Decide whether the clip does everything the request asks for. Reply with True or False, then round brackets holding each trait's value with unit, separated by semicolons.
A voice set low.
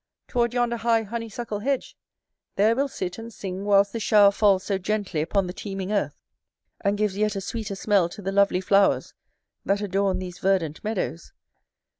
False (200 Hz)